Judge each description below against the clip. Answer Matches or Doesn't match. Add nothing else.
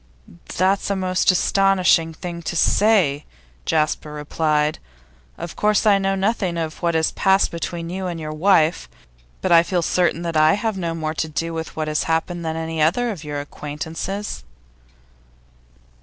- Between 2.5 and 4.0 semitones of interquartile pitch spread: Matches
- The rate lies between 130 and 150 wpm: Doesn't match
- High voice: Doesn't match